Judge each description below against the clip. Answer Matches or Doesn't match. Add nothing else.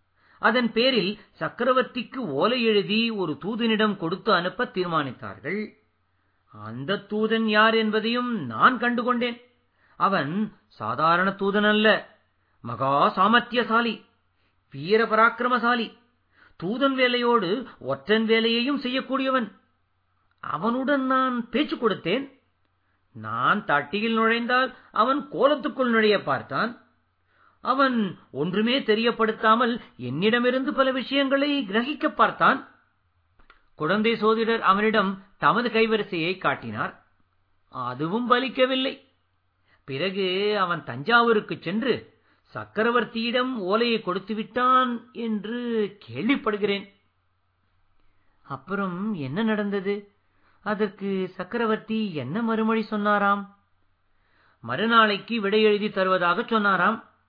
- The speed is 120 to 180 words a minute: Doesn't match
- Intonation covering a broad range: Matches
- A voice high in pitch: Matches